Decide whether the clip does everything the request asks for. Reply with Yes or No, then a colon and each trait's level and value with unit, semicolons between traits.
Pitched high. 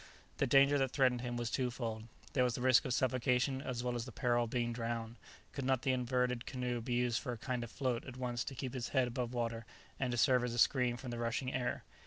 No: low, 125 Hz